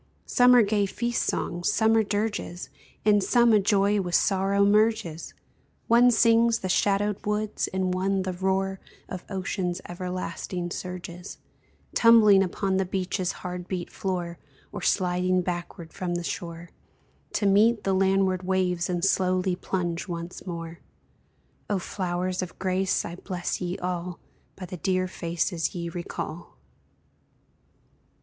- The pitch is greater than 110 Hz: Yes, medium, 185 Hz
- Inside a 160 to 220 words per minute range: No, average, 140 wpm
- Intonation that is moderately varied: No, narrow, 2.2 semitones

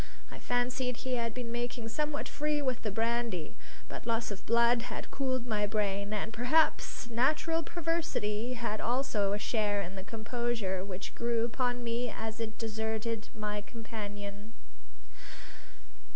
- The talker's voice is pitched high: Yes, high, 230 Hz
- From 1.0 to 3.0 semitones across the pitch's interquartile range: Yes, average, 2.7 semitones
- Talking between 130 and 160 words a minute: Yes, average, 145 wpm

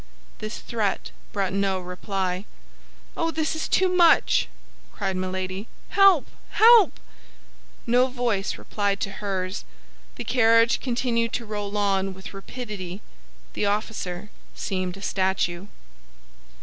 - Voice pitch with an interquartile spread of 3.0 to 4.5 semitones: Yes, average, 4.0 semitones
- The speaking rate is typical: No, slow, 115 wpm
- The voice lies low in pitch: No, high, 205 Hz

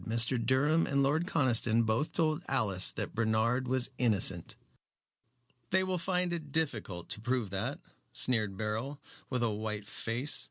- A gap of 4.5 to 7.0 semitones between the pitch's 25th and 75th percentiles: Yes, average, 4.8 semitones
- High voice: No, low, 125 Hz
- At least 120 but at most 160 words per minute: Yes, average, 150 wpm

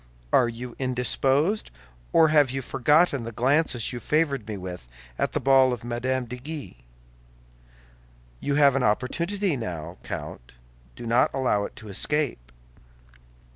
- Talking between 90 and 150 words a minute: Yes, average, 140 wpm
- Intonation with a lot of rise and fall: No, average, 3.9 semitones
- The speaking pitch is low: Yes, low, 130 Hz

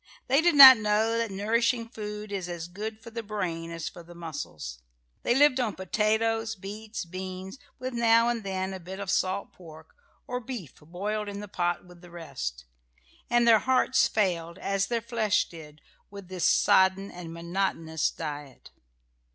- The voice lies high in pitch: Yes, high, 195 Hz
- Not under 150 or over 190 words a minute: Yes, average, 170 wpm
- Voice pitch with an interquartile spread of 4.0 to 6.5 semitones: Yes, average, 4.6 semitones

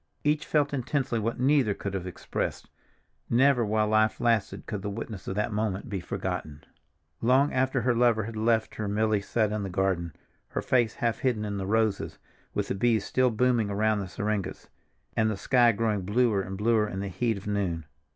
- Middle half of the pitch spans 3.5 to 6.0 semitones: No, average, 3.0 semitones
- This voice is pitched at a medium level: No, low, 110 Hz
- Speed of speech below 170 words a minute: No, average, 195 wpm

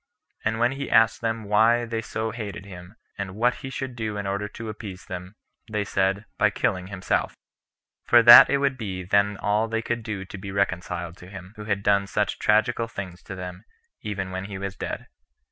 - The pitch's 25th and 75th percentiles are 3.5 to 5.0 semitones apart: No, average, 2.8 semitones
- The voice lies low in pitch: Yes, low, 105 Hz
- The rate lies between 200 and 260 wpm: Yes, fast, 205 wpm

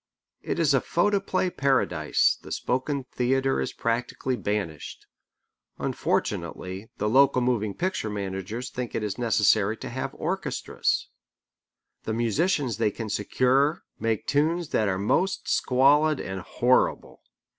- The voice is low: Yes, low, 125 Hz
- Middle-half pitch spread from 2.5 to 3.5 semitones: No, average, 4.8 semitones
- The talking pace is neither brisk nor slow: No, slow, 125 wpm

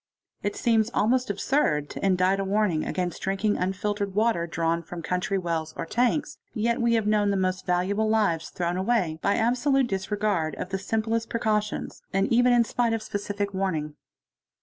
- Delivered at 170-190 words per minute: Yes, average, 175 wpm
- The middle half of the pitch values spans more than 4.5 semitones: No, average, 3.7 semitones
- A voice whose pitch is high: Yes, high, 200 Hz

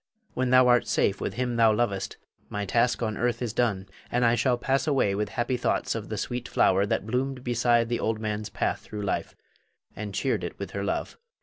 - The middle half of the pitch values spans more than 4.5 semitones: No, average, 2.7 semitones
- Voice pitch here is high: No, low, 120 Hz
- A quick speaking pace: Yes, fast, 215 wpm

